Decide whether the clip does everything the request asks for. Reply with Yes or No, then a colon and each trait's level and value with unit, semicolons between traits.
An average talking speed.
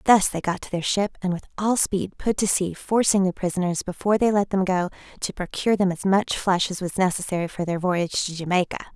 No: fast, 235 wpm